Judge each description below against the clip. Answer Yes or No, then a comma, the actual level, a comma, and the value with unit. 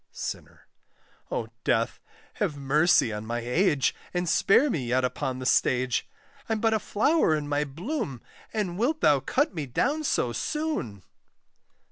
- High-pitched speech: No, medium, 150 Hz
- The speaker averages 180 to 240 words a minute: No, average, 150 wpm